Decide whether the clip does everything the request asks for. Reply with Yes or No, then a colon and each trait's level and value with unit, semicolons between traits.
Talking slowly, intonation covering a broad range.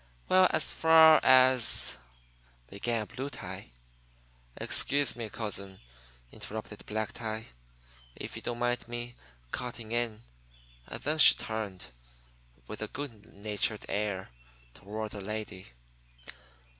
No: slow, 120 wpm; average, 3.3 semitones